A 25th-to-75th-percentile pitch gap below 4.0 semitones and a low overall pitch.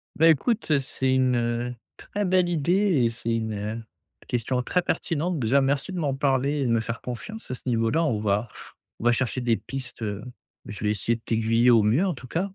No: average, 4.7 semitones; low, 125 Hz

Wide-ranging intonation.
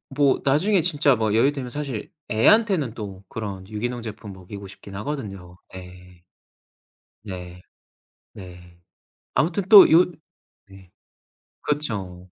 Yes: wide, 7.4 semitones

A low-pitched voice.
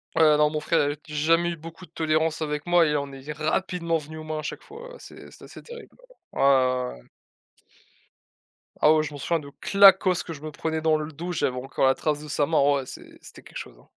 No: medium, 155 Hz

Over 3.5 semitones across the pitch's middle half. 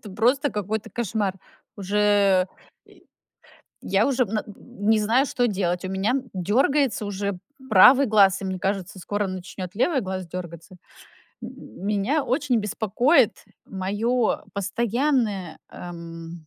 Yes: average, 4.1 semitones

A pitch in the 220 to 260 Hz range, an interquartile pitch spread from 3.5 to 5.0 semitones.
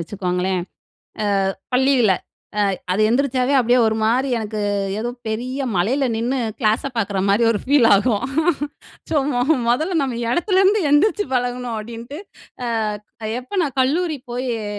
Yes: high, 245 Hz; average, 4.1 semitones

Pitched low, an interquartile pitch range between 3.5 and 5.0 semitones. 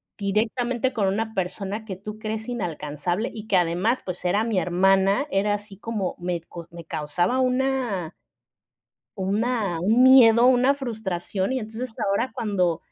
No: high, 210 Hz; average, 4.3 semitones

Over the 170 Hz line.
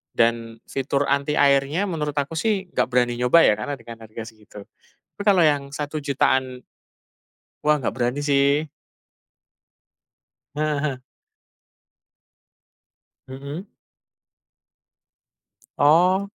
No: medium, 140 Hz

